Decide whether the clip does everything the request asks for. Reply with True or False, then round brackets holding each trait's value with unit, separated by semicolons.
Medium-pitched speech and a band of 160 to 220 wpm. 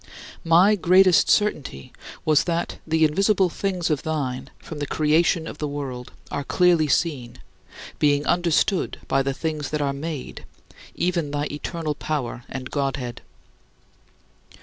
False (155 Hz; 135 wpm)